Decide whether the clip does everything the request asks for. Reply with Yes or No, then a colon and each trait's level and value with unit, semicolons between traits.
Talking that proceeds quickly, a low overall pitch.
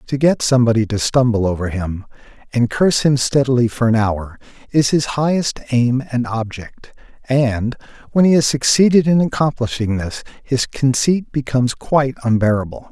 No: average, 155 wpm; low, 125 Hz